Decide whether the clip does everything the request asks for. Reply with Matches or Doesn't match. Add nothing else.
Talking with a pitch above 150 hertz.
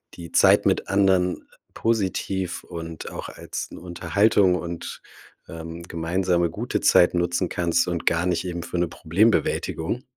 Doesn't match